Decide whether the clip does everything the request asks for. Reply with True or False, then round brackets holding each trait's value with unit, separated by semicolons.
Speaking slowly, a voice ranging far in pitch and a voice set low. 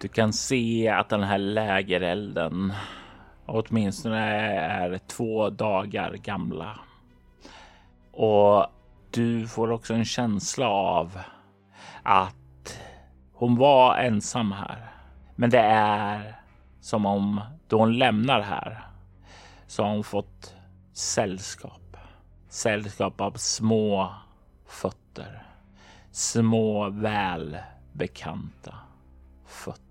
False (90 wpm; 3.2 semitones; 100 Hz)